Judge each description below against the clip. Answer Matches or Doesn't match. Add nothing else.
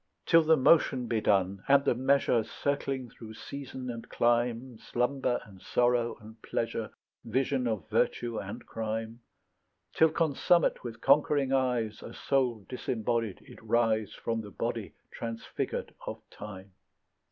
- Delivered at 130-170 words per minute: Matches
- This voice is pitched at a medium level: Doesn't match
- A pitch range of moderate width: Matches